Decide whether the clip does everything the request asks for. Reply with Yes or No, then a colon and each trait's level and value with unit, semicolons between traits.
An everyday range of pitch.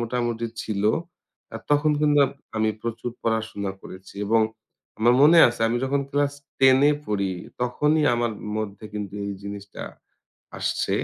Yes: average, 4.3 semitones